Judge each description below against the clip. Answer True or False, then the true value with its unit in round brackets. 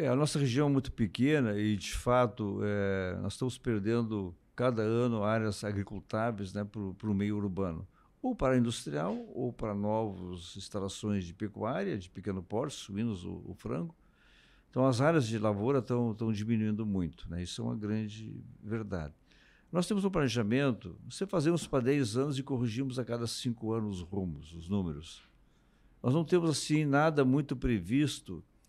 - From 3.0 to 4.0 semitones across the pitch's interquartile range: False (4.7 semitones)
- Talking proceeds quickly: False (165 wpm)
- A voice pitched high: False (110 Hz)